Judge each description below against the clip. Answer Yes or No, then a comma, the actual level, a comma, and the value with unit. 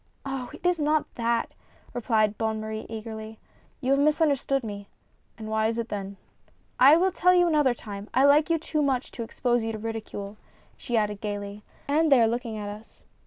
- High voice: Yes, high, 230 Hz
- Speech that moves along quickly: Yes, fast, 225 wpm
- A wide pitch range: No, average, 4.6 semitones